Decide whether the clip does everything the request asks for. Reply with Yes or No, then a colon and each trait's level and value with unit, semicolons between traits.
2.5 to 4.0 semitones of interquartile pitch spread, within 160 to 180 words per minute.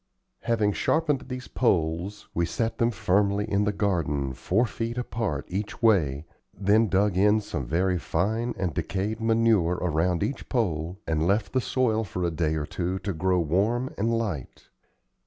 No: average, 4.7 semitones; average, 165 wpm